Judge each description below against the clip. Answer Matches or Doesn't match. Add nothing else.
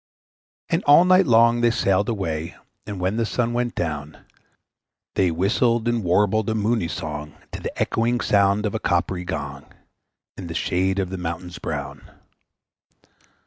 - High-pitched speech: Doesn't match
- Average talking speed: Matches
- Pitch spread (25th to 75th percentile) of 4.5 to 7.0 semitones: Matches